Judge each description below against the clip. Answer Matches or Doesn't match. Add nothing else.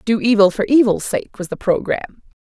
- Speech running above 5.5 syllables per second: Matches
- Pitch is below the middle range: Doesn't match